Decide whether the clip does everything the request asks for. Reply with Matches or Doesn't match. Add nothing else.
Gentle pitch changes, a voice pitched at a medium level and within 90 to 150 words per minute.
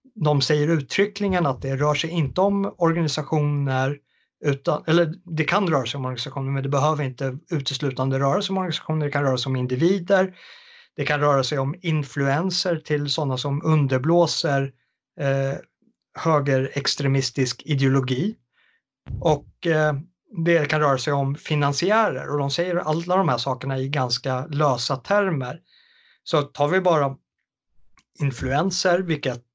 Doesn't match